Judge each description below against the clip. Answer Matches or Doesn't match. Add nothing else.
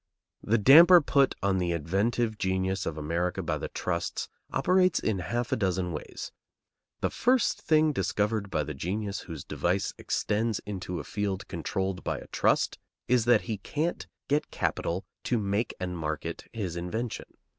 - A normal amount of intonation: Matches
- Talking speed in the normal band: Matches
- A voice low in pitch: Matches